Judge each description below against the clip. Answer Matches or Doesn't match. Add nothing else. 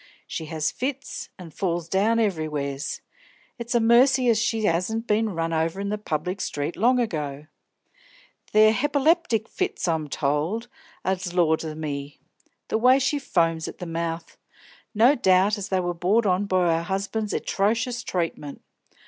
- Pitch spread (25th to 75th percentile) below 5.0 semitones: Doesn't match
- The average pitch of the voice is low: Doesn't match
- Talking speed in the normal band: Matches